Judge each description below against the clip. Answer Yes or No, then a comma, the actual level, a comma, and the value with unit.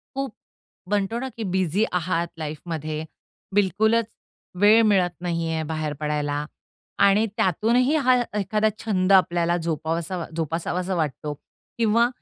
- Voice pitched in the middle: Yes, medium, 180 Hz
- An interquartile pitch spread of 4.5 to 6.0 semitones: Yes, average, 5.0 semitones